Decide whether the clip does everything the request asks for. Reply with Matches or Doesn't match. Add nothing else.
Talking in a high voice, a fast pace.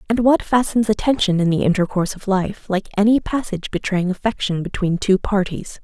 Doesn't match